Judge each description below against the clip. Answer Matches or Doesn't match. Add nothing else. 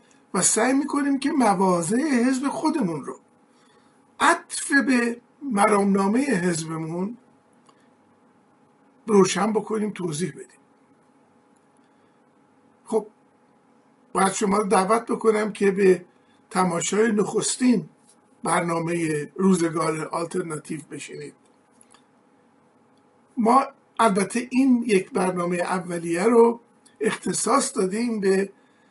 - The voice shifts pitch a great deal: Matches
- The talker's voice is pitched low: Doesn't match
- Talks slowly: Matches